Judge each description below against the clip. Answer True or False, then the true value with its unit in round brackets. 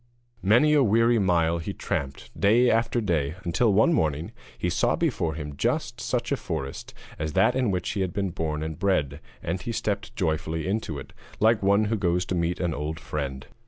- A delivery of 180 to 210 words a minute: True (195 wpm)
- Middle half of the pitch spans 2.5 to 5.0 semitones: False (5.4 semitones)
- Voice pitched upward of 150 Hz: False (90 Hz)